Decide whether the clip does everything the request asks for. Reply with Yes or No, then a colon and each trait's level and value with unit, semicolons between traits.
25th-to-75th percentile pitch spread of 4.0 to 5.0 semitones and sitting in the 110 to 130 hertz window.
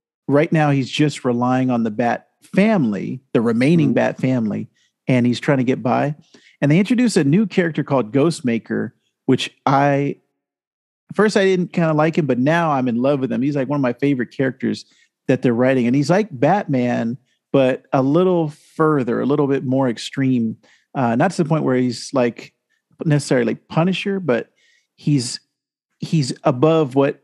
No: average, 4.4 semitones; medium, 140 Hz